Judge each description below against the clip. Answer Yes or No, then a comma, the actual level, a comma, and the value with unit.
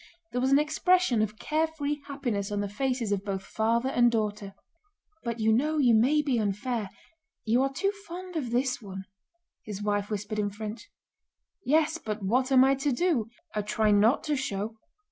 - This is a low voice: No, high, 235 Hz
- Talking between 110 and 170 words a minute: No, average, 185 wpm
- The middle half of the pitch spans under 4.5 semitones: No, average, 5.1 semitones